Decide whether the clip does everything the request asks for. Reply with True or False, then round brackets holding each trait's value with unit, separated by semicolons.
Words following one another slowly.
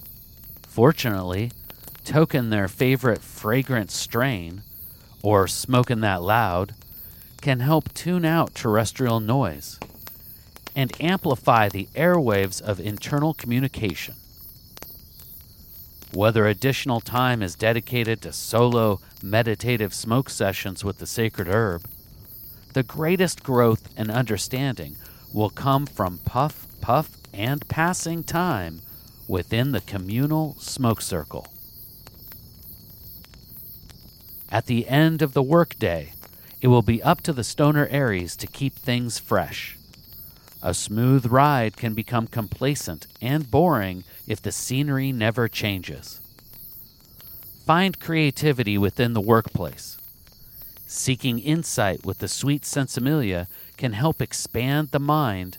True (110 wpm)